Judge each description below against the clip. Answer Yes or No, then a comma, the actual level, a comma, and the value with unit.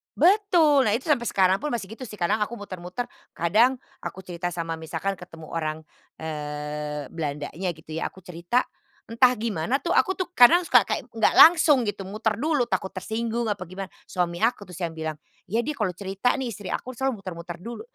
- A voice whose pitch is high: Yes, high, 200 Hz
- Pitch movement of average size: No, wide, 6.1 semitones